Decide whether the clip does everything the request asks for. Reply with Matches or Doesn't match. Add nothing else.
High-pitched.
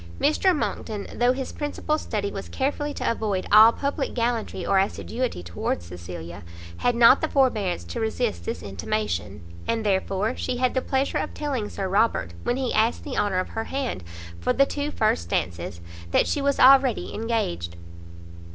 Matches